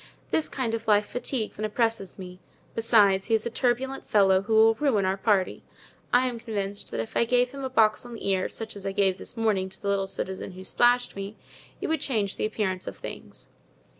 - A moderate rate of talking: No, fast, 225 wpm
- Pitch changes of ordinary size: Yes, average, 3.5 semitones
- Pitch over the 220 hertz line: No, high, 215 Hz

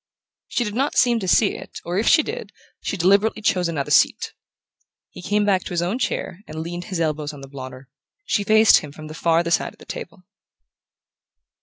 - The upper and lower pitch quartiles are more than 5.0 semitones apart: Yes, wide, 5.4 semitones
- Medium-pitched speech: Yes, medium, 180 Hz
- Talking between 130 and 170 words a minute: No, fast, 205 wpm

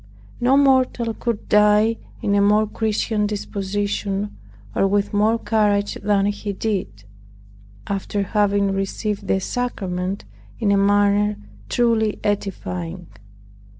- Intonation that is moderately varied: No, narrow, 1.5 semitones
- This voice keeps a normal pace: No, slow, 115 wpm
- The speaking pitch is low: No, high, 205 Hz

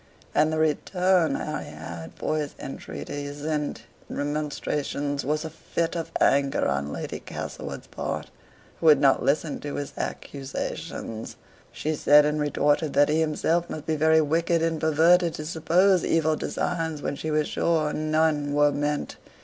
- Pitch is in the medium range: Yes, medium, 155 Hz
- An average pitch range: No, narrow, 1.8 semitones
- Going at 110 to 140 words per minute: No, average, 155 wpm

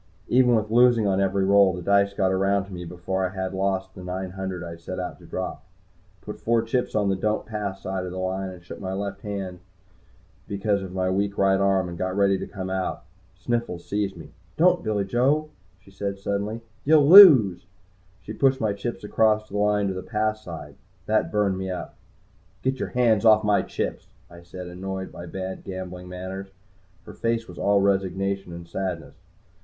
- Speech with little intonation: Yes, narrow, 2.3 semitones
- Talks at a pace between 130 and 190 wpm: No, average, 200 wpm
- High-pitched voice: No, very low, 95 Hz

